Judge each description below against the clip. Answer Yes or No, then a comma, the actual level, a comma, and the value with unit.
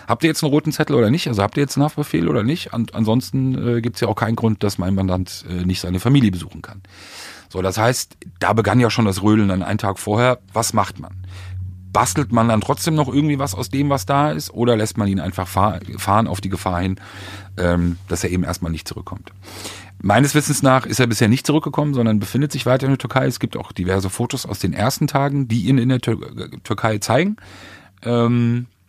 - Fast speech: Yes, fast, 235 wpm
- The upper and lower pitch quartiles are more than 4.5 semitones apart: Yes, wide, 5.4 semitones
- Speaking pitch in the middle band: No, low, 110 Hz